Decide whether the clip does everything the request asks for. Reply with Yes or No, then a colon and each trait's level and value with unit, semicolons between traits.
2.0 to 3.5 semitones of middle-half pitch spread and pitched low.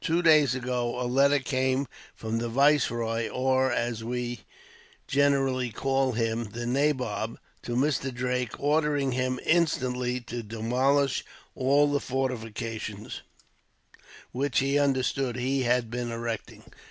Yes: narrow, 2.5 semitones; low, 125 Hz